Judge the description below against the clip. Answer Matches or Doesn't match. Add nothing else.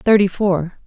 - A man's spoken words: Doesn't match